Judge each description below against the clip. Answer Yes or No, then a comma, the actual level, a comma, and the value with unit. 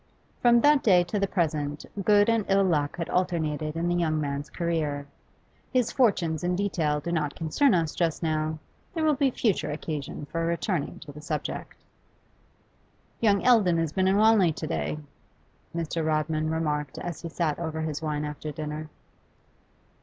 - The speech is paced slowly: No, average, 170 wpm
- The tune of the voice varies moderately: Yes, average, 3.7 semitones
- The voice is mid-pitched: Yes, medium, 165 Hz